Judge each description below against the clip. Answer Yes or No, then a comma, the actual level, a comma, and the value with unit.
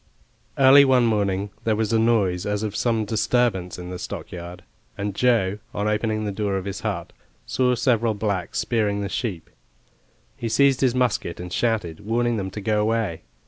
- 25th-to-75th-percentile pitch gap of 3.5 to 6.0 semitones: No, average, 3.1 semitones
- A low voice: Yes, low, 105 Hz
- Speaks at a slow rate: No, average, 180 wpm